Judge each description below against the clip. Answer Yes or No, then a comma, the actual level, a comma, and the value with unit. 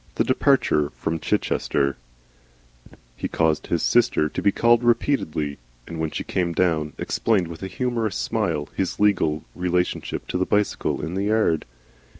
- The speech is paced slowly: No, average, 150 wpm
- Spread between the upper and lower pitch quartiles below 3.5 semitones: No, average, 4.8 semitones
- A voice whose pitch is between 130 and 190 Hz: No, very low, 90 Hz